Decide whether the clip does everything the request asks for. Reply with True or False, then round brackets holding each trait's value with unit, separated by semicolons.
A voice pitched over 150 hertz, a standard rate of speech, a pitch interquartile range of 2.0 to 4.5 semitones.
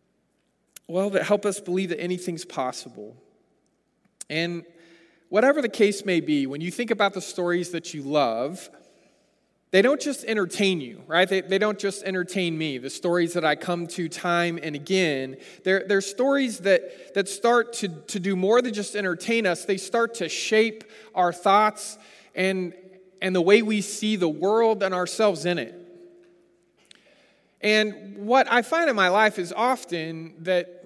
True (190 Hz; 175 wpm; 3.5 semitones)